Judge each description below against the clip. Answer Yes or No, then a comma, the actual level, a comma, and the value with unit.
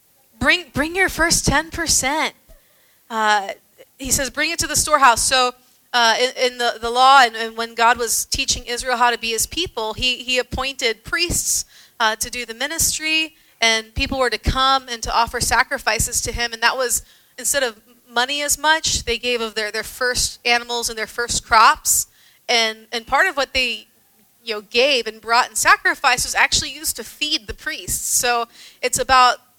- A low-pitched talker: No, high, 245 Hz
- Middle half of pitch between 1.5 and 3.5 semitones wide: Yes, average, 3.1 semitones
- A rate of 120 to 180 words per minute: No, average, 195 wpm